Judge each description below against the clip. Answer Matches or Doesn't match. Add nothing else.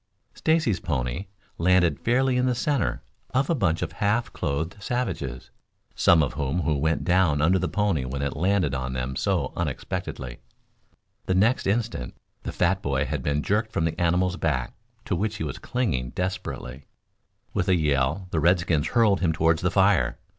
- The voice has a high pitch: Doesn't match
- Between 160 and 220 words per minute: Matches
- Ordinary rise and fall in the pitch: Doesn't match